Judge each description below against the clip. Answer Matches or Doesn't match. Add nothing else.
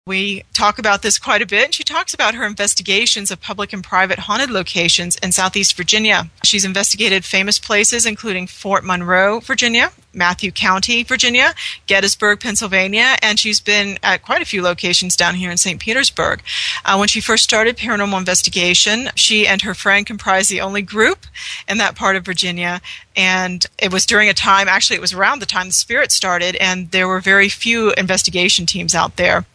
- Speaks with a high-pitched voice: Matches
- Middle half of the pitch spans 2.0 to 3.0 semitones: Matches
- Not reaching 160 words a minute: Doesn't match